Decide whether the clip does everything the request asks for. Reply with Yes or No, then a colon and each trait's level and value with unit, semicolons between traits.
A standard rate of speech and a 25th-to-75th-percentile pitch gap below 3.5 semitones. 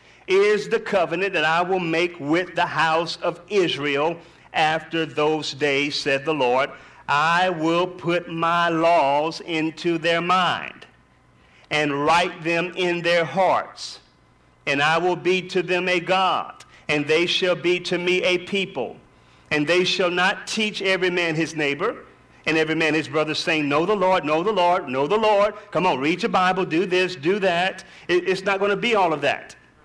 Yes: average, 180 wpm; narrow, 2.6 semitones